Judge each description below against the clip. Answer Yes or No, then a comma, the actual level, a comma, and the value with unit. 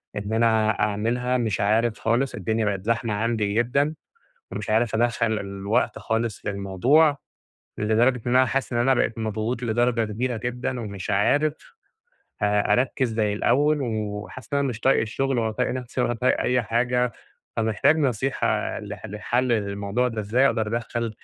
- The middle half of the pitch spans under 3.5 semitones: Yes, average, 2.7 semitones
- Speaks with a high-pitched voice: No, low, 115 Hz